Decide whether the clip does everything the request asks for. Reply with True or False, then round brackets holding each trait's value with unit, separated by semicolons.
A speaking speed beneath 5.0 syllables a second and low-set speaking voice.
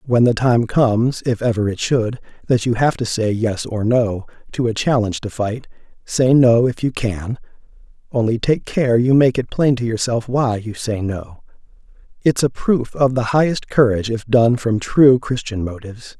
True (4.7 syllables/s; 120 Hz)